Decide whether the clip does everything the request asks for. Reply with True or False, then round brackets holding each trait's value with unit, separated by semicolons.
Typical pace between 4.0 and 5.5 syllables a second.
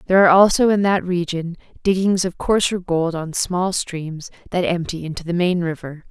True (5.1 syllables/s)